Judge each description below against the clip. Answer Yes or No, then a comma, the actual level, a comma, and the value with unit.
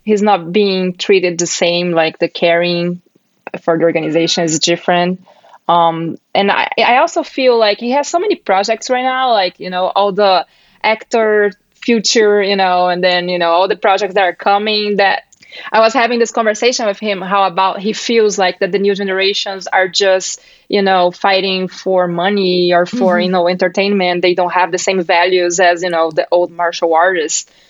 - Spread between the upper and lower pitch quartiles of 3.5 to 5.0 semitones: No, average, 2.7 semitones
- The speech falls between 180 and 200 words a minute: Yes, average, 195 wpm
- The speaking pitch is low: No, high, 190 Hz